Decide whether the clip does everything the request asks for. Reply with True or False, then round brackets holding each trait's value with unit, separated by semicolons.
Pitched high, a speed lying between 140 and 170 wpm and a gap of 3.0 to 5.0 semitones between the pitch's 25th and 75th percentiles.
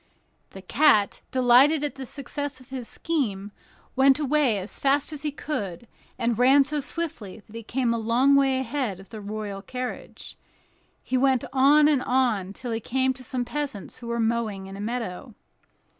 False (250 Hz; 180 wpm; 4.1 semitones)